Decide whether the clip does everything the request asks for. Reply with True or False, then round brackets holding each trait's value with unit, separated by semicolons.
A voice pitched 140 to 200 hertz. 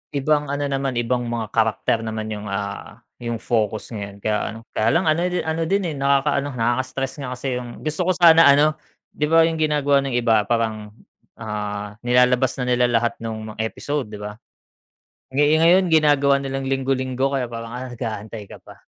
False (125 Hz)